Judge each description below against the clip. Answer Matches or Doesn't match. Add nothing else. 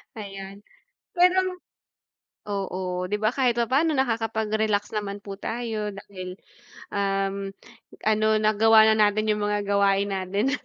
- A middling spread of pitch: Doesn't match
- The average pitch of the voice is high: Matches